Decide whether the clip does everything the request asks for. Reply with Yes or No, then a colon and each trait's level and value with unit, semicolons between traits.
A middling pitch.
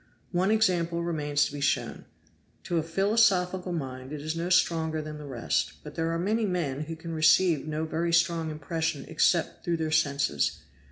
Yes: medium, 165 Hz